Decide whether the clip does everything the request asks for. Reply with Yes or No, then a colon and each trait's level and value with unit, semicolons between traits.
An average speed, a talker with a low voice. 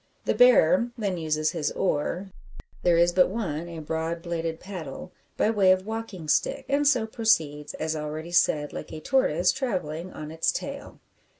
No: average, 170 wpm; medium, 170 Hz